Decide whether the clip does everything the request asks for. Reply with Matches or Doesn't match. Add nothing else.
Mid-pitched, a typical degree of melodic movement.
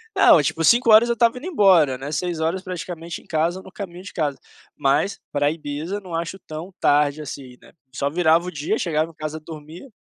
Matches